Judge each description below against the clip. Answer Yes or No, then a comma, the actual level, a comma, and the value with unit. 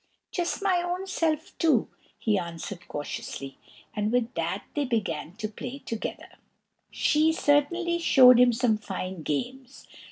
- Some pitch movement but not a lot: No, wide, 7.6 semitones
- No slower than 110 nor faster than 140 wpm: Yes, slow, 135 wpm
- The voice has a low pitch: No, high, 245 Hz